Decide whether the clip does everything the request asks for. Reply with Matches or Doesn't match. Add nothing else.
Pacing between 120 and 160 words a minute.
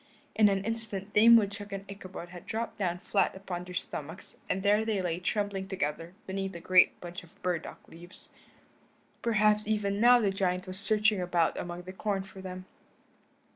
Doesn't match